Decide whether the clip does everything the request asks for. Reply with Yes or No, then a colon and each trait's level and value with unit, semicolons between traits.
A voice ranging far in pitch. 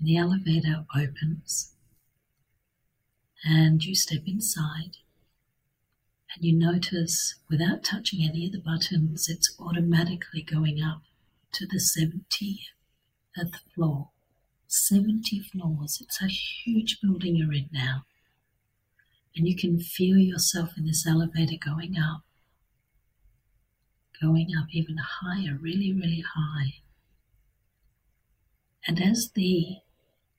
No: average, 5.0 semitones